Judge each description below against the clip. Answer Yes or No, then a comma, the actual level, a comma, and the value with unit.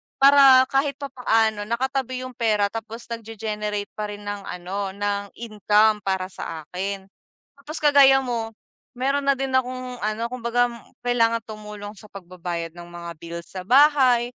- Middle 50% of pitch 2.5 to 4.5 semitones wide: Yes, average, 4.1 semitones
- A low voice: No, high, 225 Hz